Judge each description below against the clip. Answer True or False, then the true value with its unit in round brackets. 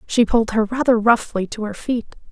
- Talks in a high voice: True (225 Hz)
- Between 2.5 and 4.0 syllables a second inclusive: False (5.4 syllables/s)